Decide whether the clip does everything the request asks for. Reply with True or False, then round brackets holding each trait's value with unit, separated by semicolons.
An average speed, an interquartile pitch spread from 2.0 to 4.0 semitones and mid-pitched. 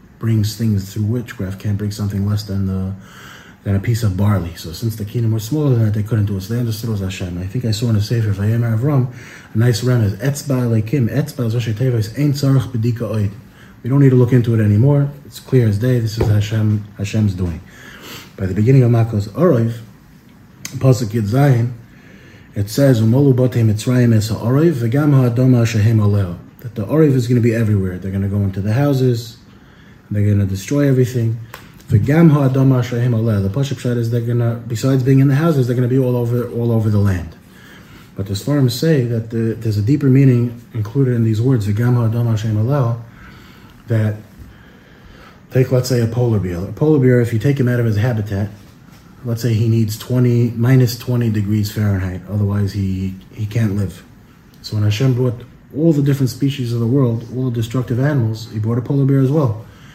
False (185 wpm; 3.3 semitones; 115 Hz)